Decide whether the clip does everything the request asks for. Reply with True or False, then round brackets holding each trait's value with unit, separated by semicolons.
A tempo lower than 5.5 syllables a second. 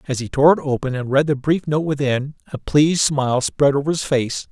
False (5.6 syllables/s)